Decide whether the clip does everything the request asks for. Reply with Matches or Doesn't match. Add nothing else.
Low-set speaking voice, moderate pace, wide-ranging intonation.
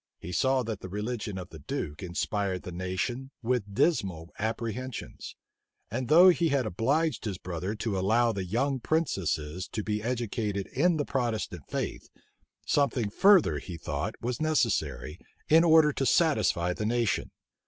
Matches